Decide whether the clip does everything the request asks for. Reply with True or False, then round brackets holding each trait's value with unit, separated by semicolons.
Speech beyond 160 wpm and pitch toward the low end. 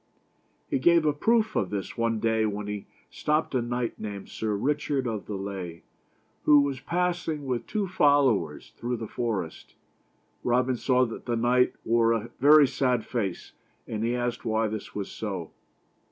True (170 wpm; 120 Hz)